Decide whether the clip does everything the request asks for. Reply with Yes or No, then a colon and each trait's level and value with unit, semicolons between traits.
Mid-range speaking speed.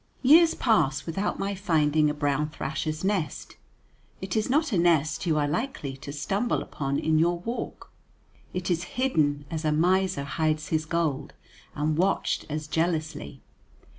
Yes: average, 155 wpm